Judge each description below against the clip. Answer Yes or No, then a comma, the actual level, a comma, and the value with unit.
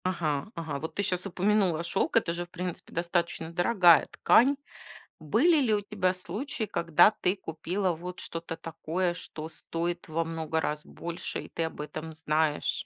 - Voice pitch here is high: No, medium, 170 Hz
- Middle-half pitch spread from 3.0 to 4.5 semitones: No, narrow, 2.6 semitones